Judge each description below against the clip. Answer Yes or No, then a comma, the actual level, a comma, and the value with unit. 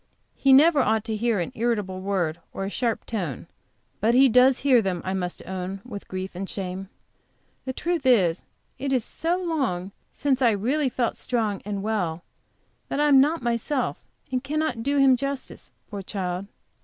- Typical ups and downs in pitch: No, wide, 5.8 semitones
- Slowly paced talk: No, average, 180 wpm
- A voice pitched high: Yes, high, 230 Hz